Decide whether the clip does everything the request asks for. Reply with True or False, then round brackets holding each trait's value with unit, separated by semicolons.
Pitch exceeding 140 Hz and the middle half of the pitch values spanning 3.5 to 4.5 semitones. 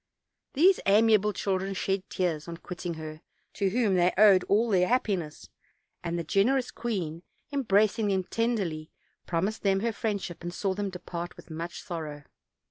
True (190 Hz; 3.8 semitones)